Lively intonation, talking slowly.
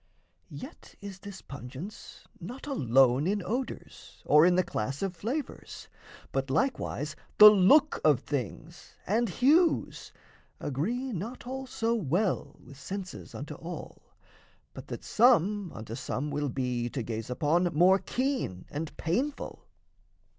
Yes: wide, 8.7 semitones; slow, 130 wpm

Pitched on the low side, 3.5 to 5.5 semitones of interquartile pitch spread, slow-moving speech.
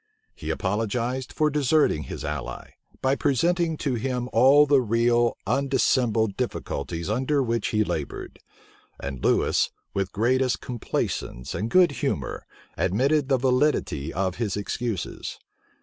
Yes: low, 120 Hz; average, 4.7 semitones; slow, 130 wpm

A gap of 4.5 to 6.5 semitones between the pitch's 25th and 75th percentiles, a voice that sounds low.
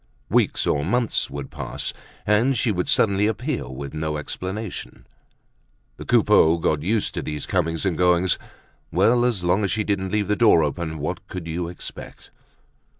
Yes: average, 5.0 semitones; very low, 90 Hz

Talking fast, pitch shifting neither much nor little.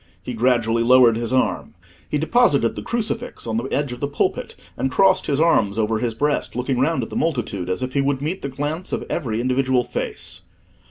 Yes: fast, 210 wpm; average, 4.1 semitones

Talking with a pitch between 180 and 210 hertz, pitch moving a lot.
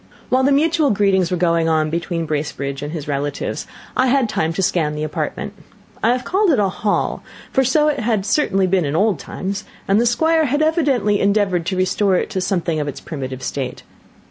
Yes: high, 190 Hz; wide, 7.5 semitones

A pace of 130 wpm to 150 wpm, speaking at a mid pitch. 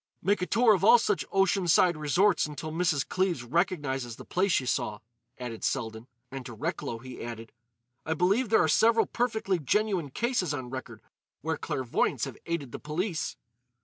No: average, 175 wpm; medium, 165 Hz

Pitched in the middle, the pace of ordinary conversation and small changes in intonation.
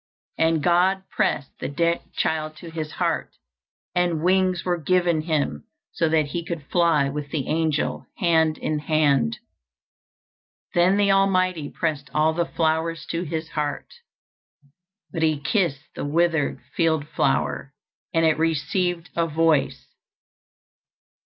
No: medium, 160 Hz; slow, 130 wpm; narrow, 2.3 semitones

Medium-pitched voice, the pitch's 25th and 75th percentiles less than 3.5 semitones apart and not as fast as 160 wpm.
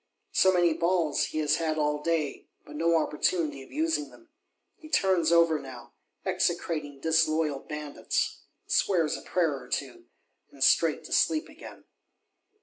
Yes: medium, 160 Hz; average, 3.1 semitones; average, 145 wpm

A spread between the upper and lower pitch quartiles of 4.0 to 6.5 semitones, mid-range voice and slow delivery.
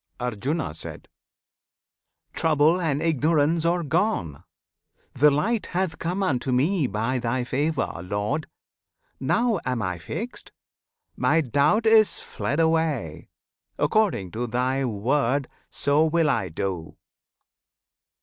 Yes: wide, 5.4 semitones; medium, 145 Hz; slow, 110 wpm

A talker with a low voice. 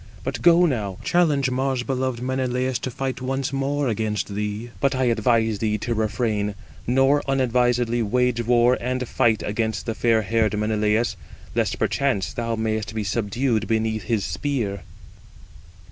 Yes: low, 120 Hz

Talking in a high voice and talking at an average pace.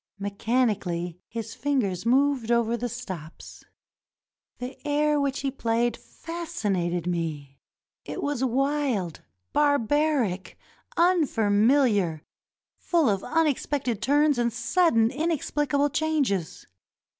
No: high, 245 Hz; slow, 100 wpm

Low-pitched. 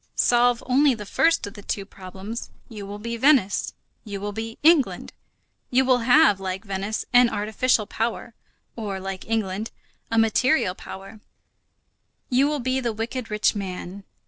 No: high, 225 Hz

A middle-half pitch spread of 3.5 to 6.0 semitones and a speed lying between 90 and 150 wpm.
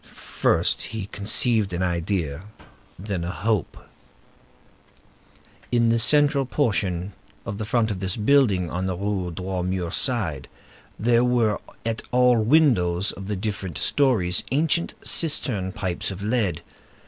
Yes: average, 4.6 semitones; slow, 135 wpm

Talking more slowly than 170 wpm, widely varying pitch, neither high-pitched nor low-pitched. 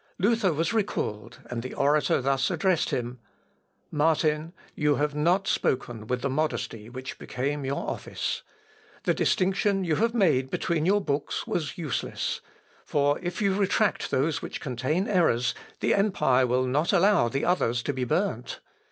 Yes: average, 155 wpm; wide, 6.2 semitones; medium, 150 Hz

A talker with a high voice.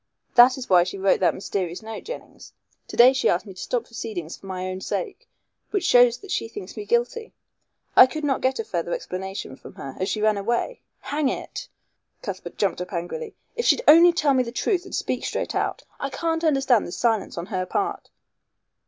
Yes: high, 235 Hz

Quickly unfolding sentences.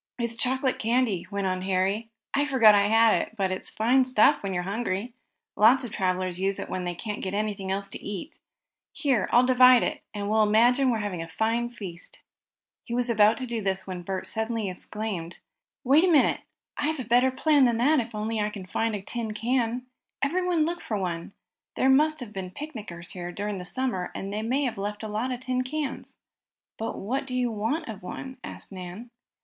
Yes: fast, 210 wpm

